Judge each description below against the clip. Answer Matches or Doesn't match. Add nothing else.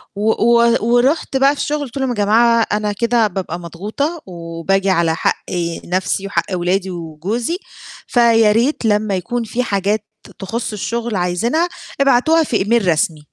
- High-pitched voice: Matches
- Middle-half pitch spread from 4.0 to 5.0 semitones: Matches